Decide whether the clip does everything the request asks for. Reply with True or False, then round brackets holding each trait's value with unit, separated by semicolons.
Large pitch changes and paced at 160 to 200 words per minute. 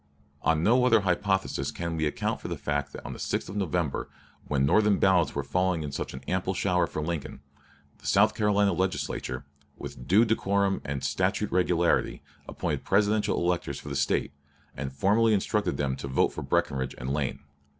True (5.8 semitones; 180 wpm)